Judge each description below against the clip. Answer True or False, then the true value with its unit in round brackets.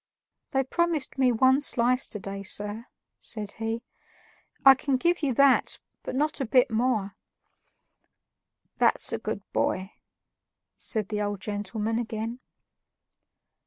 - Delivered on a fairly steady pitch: False (4.1 semitones)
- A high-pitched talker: True (235 Hz)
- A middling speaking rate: False (125 wpm)